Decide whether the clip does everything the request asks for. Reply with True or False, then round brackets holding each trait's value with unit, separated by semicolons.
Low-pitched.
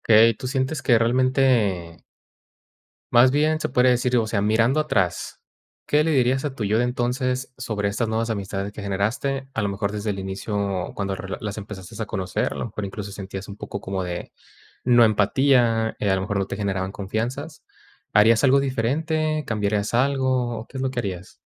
True (115 Hz)